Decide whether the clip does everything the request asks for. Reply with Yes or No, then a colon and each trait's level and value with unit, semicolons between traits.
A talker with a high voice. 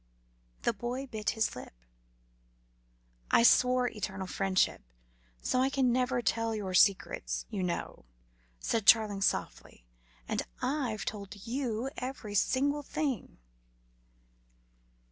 Yes: high, 230 Hz